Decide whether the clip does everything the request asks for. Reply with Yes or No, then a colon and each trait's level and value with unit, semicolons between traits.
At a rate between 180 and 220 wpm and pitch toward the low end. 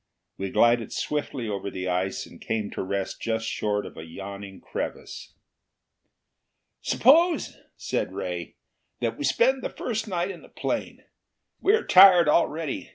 No: average, 150 wpm; low, 115 Hz